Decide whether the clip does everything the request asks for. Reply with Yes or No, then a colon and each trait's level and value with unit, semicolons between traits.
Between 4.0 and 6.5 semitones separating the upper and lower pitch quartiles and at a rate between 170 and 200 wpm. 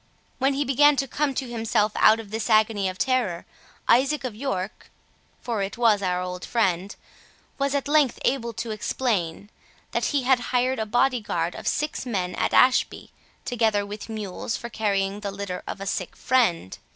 Yes: average, 4.5 semitones; average, 180 wpm